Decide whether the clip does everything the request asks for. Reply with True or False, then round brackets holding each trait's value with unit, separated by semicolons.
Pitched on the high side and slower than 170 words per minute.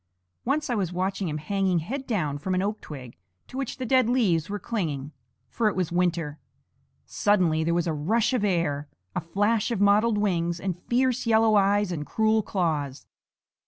False (195 Hz; 185 wpm)